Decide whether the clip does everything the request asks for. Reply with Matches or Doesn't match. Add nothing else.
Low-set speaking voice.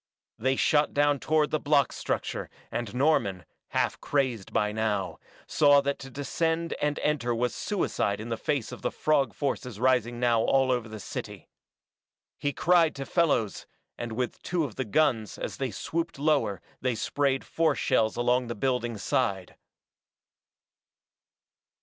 Matches